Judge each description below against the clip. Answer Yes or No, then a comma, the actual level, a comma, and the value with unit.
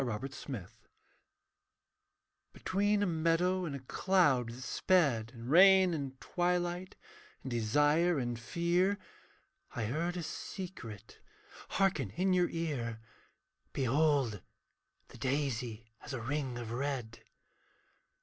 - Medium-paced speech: No, slow, 110 wpm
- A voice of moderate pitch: Yes, medium, 145 Hz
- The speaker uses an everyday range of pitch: No, wide, 6.7 semitones